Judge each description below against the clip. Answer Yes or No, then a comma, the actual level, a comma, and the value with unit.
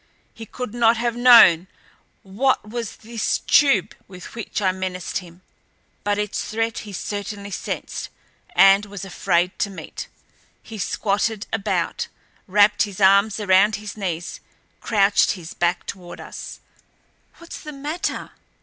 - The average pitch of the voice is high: Yes, high, 205 Hz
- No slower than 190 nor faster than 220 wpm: No, slow, 135 wpm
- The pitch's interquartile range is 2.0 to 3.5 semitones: Yes, average, 3.0 semitones